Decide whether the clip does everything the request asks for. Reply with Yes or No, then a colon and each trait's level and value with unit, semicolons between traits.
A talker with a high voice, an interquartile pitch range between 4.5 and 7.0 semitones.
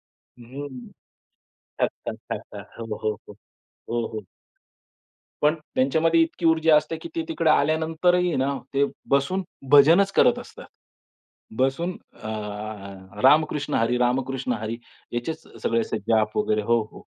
No: medium, 140 Hz; average, 5.2 semitones